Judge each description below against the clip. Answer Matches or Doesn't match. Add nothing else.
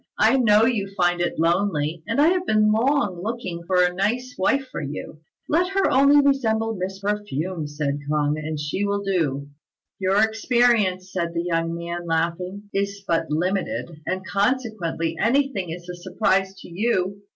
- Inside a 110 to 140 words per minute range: Doesn't match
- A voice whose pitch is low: Doesn't match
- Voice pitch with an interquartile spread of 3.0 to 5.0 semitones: Matches